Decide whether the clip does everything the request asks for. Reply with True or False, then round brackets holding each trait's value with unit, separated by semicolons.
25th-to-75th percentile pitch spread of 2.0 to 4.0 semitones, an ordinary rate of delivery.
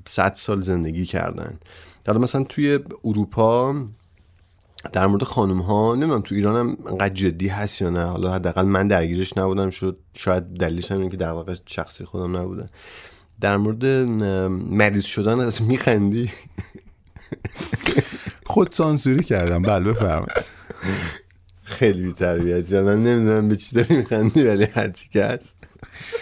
True (3.6 semitones; 140 wpm)